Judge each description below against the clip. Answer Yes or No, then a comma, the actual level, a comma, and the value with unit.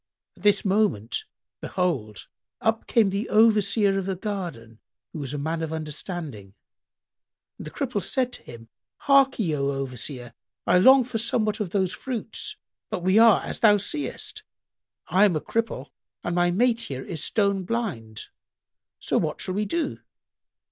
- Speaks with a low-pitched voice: No, high, 190 Hz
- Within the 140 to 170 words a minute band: Yes, average, 160 wpm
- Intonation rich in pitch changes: Yes, wide, 6.7 semitones